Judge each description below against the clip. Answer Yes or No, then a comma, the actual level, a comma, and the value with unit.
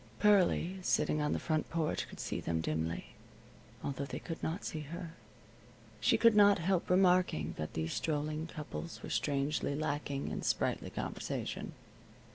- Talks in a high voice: No, medium, 155 Hz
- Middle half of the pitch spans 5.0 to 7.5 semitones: No, average, 4.3 semitones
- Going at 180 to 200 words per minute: No, average, 145 wpm